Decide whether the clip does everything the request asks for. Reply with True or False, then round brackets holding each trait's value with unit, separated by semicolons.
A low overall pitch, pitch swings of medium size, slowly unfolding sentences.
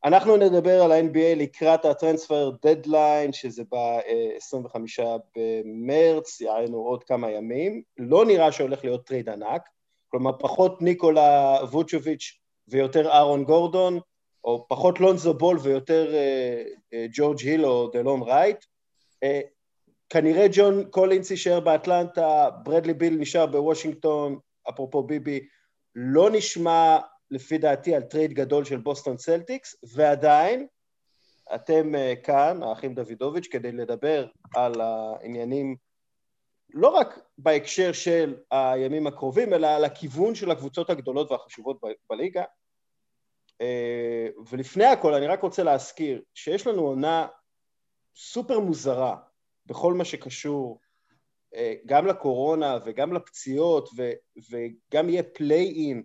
False (150 Hz; 4.5 semitones; 115 wpm)